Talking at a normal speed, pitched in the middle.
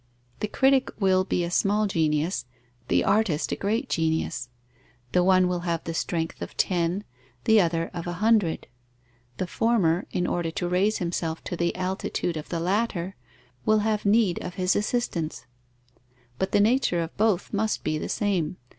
Yes: average, 170 wpm; medium, 180 Hz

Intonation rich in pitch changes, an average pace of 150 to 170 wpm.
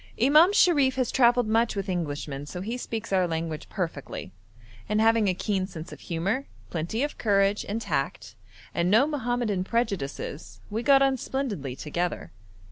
Yes: wide, 5.9 semitones; average, 160 wpm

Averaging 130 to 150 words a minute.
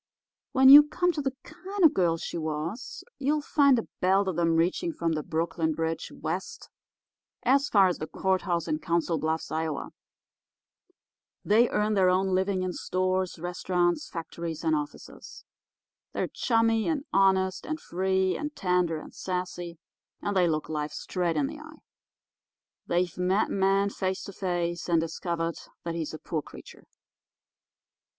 No: average, 160 wpm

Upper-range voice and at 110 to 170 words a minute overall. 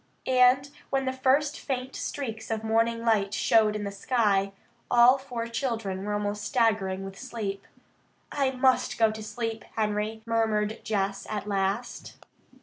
Yes: high, 225 Hz; average, 145 wpm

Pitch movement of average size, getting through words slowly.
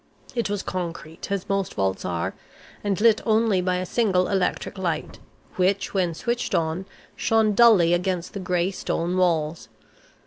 No: average, 3.1 semitones; average, 150 wpm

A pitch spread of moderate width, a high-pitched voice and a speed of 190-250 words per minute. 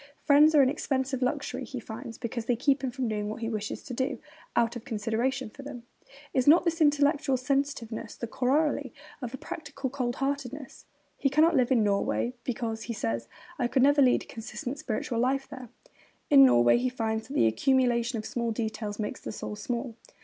Yes: average, 3.3 semitones; very high, 250 Hz; average, 195 wpm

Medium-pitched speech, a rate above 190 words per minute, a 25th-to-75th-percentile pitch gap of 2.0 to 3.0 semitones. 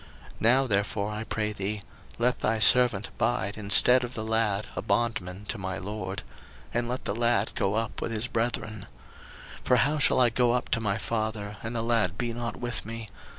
No: low, 110 Hz; average, 200 wpm; narrow, 2.6 semitones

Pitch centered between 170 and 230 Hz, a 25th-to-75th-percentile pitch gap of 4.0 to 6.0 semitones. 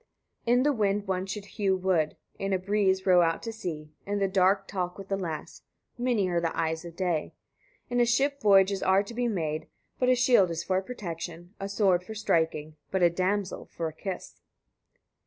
No: high, 190 Hz; average, 3.1 semitones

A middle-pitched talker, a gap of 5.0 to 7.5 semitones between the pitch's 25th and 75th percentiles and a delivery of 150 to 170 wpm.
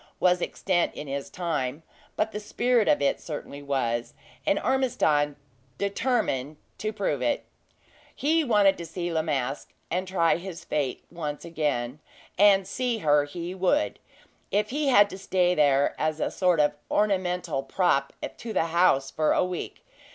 Yes: medium, 175 Hz; wide, 5.4 semitones; average, 160 wpm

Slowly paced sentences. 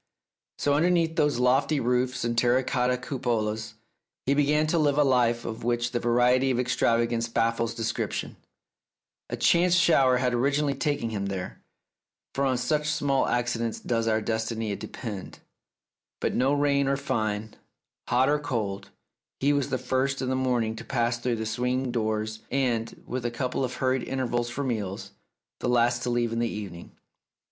No: average, 170 wpm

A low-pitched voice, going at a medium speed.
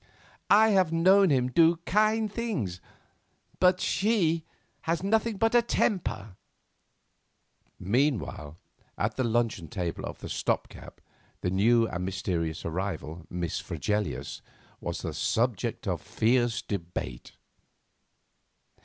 No: low, 120 Hz; slow, 115 wpm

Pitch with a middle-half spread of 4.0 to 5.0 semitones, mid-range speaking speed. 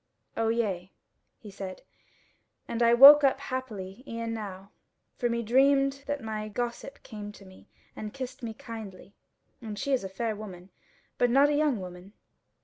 Yes: average, 4.3 semitones; average, 165 wpm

